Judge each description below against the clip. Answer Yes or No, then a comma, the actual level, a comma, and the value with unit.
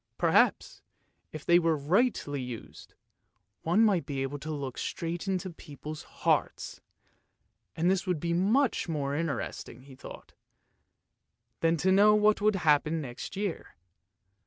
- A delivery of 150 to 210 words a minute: No, slow, 135 wpm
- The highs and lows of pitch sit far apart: No, average, 4.7 semitones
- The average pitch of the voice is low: No, medium, 165 Hz